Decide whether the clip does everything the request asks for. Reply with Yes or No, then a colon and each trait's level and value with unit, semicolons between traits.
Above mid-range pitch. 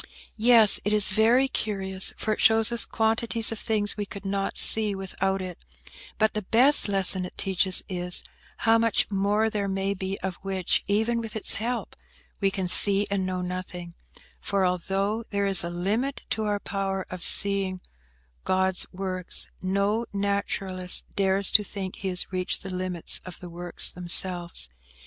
Yes: high, 195 Hz